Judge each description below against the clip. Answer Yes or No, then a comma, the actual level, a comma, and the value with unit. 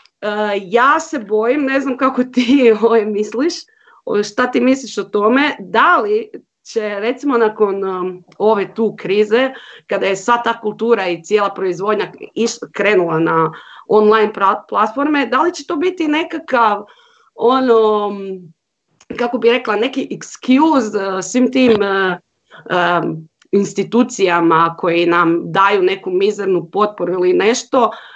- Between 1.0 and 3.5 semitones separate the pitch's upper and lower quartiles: No, average, 4.8 semitones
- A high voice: Yes, high, 215 Hz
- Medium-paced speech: Yes, average, 120 wpm